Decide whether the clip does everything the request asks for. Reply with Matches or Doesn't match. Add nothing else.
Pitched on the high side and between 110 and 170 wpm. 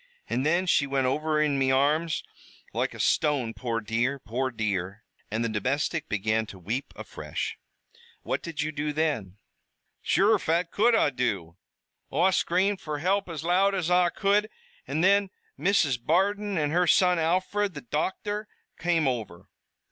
Doesn't match